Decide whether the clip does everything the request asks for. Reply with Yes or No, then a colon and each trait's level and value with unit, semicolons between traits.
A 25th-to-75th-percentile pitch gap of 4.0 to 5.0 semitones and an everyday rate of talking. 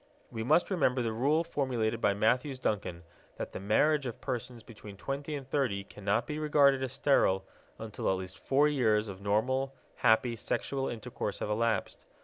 Yes: average, 4.5 semitones; average, 170 wpm